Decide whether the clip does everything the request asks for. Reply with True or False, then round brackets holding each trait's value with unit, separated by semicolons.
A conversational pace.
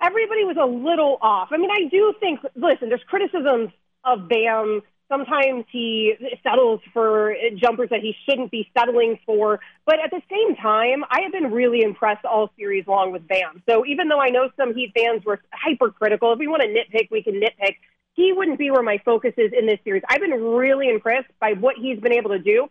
False (210 wpm)